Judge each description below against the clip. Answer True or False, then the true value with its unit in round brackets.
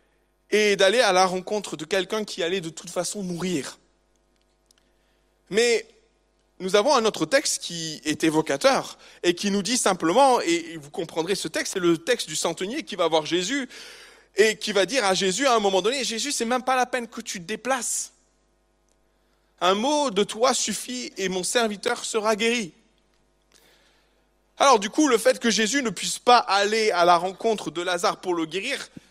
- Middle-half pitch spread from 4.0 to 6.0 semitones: True (5.5 semitones)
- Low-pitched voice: False (200 Hz)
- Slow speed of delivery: False (185 wpm)